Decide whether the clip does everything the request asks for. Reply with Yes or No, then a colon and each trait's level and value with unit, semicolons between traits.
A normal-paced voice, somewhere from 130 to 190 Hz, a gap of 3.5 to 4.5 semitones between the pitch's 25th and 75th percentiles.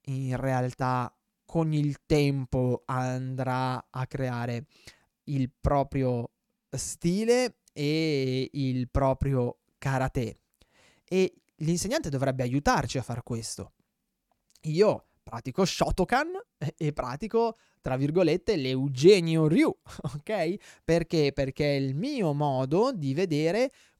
No: slow, 100 wpm; medium, 140 Hz; average, 4.2 semitones